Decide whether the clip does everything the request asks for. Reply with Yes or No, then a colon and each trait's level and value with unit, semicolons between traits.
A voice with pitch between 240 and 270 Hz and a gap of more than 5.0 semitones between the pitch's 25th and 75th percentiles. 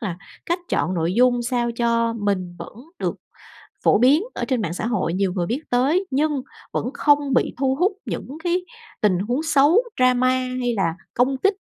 Yes: high, 245 Hz; wide, 5.4 semitones